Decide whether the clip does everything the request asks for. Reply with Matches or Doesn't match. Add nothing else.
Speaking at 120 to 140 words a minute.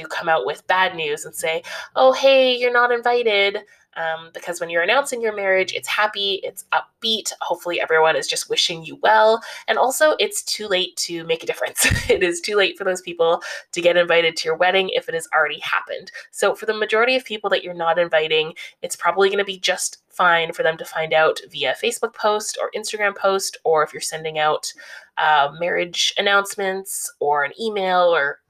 Doesn't match